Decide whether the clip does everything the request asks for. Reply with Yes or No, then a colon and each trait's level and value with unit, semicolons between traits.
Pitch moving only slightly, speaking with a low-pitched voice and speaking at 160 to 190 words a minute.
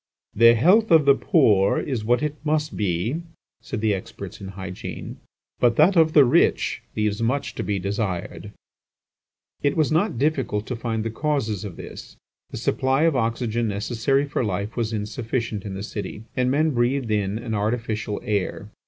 No: average, 5.1 semitones; low, 115 Hz; average, 170 wpm